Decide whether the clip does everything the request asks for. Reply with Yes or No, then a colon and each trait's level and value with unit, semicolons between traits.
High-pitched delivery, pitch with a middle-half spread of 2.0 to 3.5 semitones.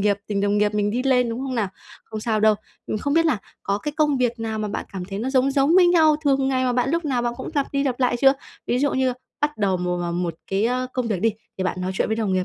No: high, 240 Hz; average, 4.7 semitones